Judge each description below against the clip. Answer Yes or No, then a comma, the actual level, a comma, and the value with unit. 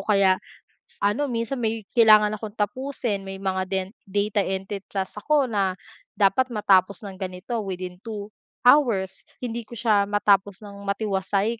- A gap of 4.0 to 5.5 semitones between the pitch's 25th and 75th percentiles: No, average, 2.7 semitones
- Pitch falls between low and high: No, high, 205 Hz